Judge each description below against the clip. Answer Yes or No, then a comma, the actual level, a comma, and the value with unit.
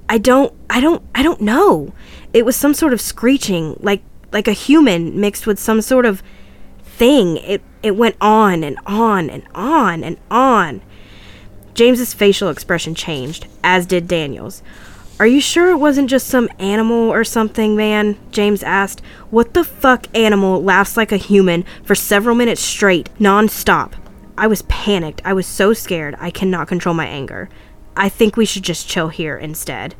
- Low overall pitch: No, high, 205 Hz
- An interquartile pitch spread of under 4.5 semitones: No, average, 4.8 semitones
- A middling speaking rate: Yes, average, 170 wpm